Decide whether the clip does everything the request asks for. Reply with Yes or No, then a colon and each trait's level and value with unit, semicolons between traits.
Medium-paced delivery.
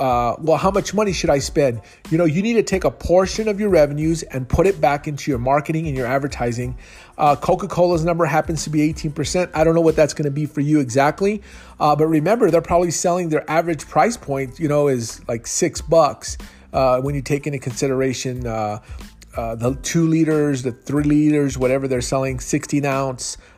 No: fast, 210 wpm